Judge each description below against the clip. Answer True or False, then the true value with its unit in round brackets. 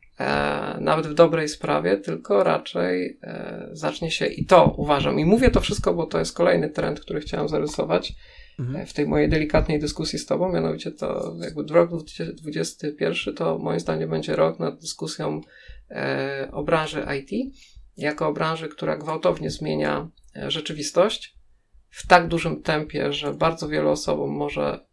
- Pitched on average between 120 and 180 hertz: True (135 Hz)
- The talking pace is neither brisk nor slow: True (145 wpm)